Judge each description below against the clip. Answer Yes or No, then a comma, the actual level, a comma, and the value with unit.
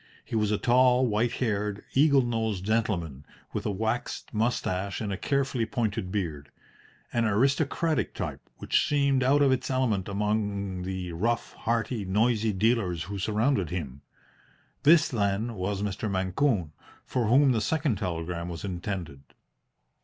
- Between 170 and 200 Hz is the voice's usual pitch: No, low, 105 Hz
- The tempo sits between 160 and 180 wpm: No, average, 145 wpm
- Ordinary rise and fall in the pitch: Yes, average, 4.5 semitones